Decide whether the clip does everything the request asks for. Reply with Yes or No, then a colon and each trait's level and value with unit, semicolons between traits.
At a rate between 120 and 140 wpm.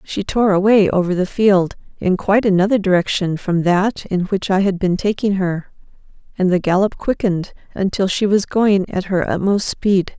No: average, 185 wpm